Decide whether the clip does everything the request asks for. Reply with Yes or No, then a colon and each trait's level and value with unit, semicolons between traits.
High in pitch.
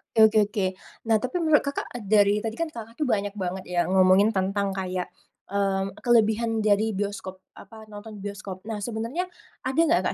Yes: high, 210 Hz